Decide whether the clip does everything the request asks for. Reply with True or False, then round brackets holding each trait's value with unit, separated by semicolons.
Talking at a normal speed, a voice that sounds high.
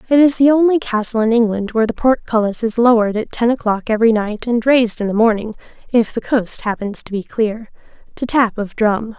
False (215 wpm; 230 Hz)